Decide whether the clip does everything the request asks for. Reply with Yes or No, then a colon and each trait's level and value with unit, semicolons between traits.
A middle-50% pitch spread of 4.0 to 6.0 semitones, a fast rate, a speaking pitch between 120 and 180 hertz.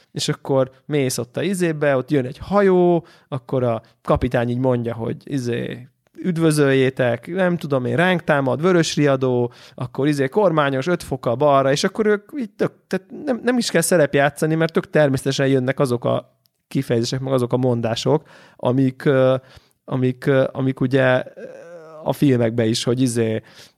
Yes: average, 4.4 semitones; fast, 160 wpm; low, 135 Hz